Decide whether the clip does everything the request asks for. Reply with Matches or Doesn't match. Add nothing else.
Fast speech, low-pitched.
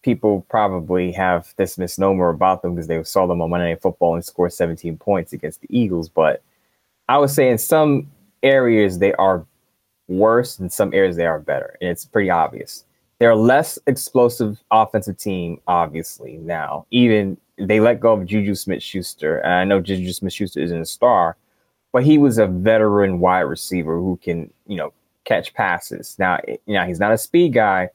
Doesn't match